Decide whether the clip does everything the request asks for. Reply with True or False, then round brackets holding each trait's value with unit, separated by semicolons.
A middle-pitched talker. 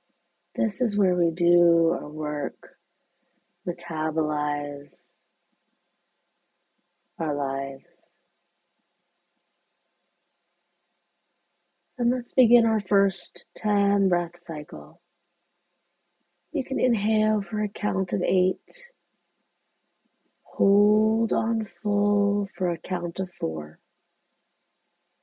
True (175 Hz)